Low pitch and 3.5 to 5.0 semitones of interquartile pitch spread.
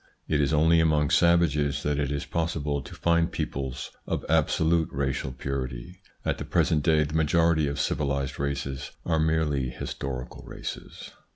No: very low, 75 Hz; average, 2.7 semitones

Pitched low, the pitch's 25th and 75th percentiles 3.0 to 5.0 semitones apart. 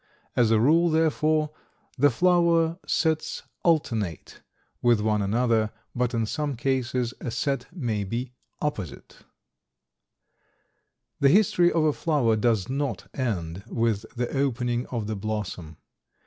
No: low, 125 Hz; wide, 5.6 semitones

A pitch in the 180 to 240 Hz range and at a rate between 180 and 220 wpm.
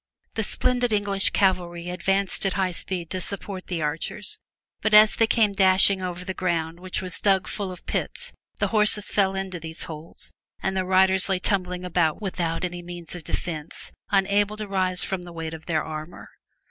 Yes: medium, 185 Hz; average, 185 wpm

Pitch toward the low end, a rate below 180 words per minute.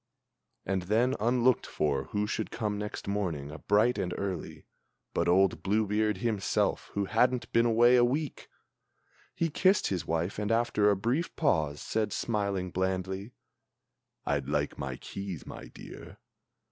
Yes: low, 105 Hz; average, 145 wpm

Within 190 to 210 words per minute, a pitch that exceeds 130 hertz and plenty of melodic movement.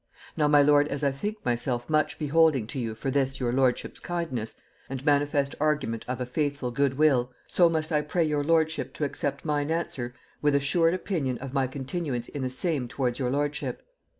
No: average, 195 wpm; medium, 140 Hz; average, 2.9 semitones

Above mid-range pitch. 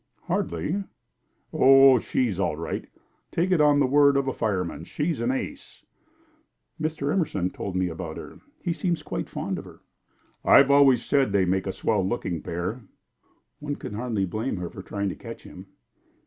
No: low, 120 Hz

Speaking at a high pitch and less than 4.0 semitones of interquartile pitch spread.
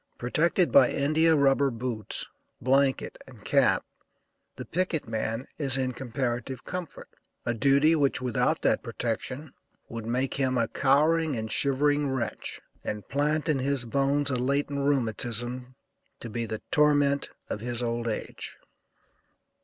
No: low, 135 Hz; average, 3.1 semitones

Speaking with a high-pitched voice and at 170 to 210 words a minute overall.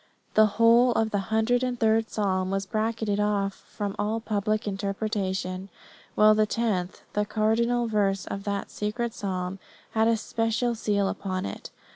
No: high, 215 Hz; average, 160 wpm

